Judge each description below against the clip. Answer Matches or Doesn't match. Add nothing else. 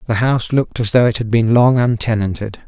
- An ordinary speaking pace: Doesn't match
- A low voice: Matches